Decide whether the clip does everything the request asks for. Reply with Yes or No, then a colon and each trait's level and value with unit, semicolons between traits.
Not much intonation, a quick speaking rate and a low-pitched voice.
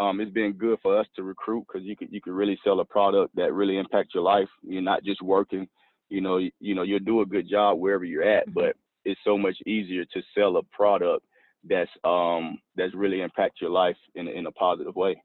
Yes: narrow, 1.7 semitones; fast, 235 wpm; low, 100 Hz